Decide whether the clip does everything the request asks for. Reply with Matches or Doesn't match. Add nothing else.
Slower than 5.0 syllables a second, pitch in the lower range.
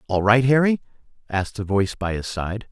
Doesn't match